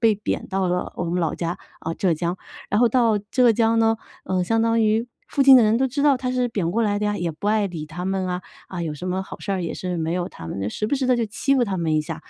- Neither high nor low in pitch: No, high, 205 Hz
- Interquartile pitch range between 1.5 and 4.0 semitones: No, average, 4.6 semitones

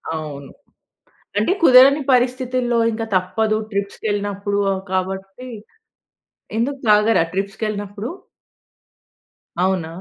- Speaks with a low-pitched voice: No, high, 205 Hz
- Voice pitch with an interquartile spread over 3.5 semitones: Yes, average, 3.9 semitones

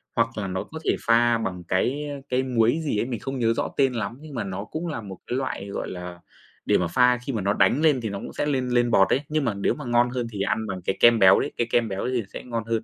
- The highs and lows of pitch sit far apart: No, average, 4.2 semitones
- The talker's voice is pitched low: Yes, low, 115 Hz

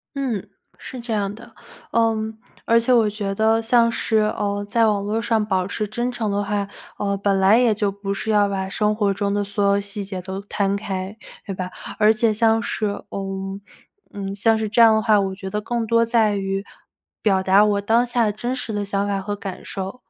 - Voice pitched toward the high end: Yes, high, 205 Hz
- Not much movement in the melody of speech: Yes, narrow, 2.1 semitones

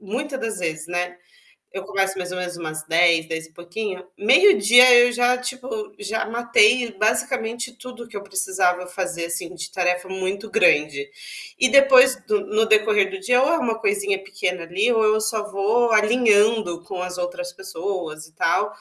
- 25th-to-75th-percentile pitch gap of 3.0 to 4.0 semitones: No, average, 4.8 semitones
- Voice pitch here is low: No, high, 205 Hz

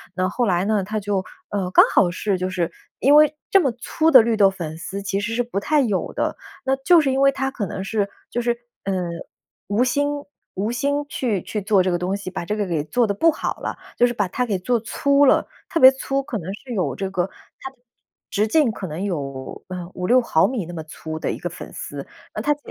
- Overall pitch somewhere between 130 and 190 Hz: No, high, 210 Hz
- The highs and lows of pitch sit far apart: Yes, wide, 6.0 semitones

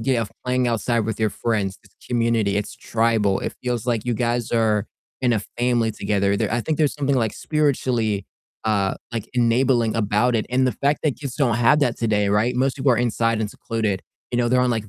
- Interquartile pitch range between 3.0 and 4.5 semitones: No, narrow, 2.5 semitones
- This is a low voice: Yes, low, 115 Hz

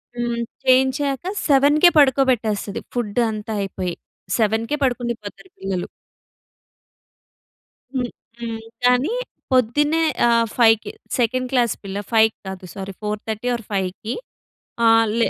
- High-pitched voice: Yes, high, 235 Hz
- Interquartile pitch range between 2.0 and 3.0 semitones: No, average, 3.4 semitones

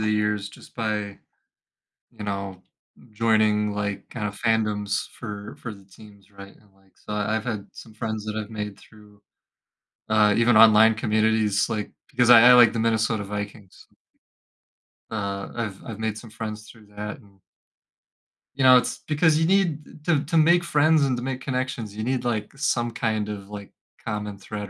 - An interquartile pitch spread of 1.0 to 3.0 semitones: Yes, narrow, 2.4 semitones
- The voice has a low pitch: Yes, low, 110 Hz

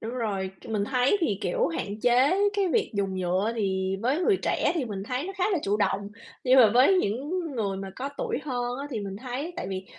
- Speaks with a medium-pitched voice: No, high, 230 Hz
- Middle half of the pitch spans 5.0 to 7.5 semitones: Yes, wide, 5.5 semitones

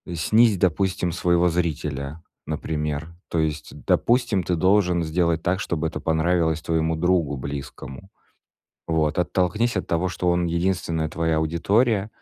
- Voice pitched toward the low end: Yes, very low, 85 Hz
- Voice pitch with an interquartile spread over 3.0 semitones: No, narrow, 2.6 semitones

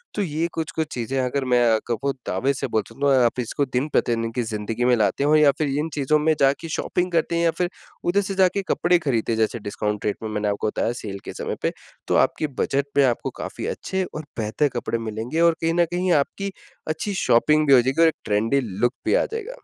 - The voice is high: No, medium, 140 Hz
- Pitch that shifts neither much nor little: No, wide, 6.1 semitones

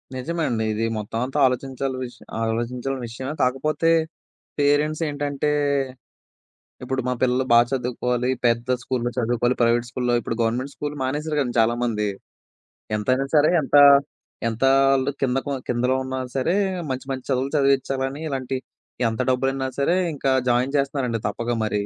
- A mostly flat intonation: Yes, narrow, 2.2 semitones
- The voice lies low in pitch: Yes, low, 130 Hz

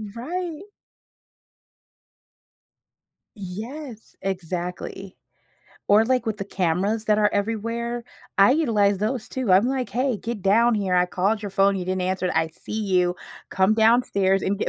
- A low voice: No, high, 205 Hz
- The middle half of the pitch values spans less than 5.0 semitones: Yes, average, 3.8 semitones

